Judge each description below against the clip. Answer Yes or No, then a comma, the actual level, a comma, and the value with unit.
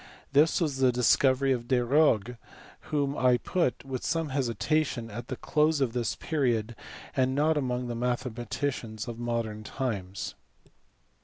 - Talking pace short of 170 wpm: Yes, average, 140 wpm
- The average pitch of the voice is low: Yes, low, 125 Hz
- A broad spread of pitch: No, average, 3.1 semitones